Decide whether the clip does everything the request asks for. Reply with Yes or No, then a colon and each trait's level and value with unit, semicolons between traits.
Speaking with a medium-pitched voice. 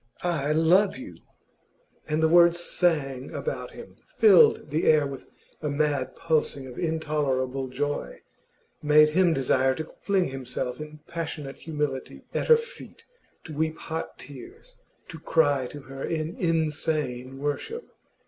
Yes: medium, 155 Hz